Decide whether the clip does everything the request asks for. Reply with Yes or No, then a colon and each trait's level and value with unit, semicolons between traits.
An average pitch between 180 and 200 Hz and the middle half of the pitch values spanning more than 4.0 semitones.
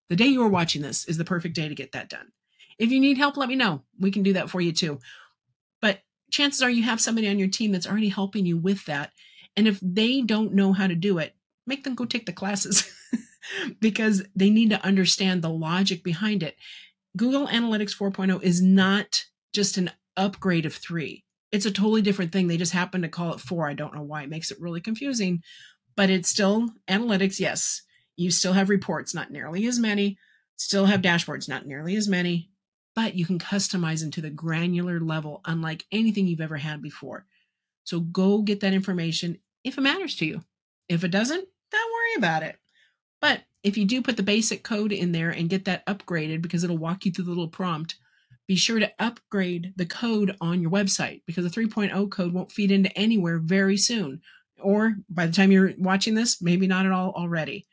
No: high, 190 Hz; average, 3.4 semitones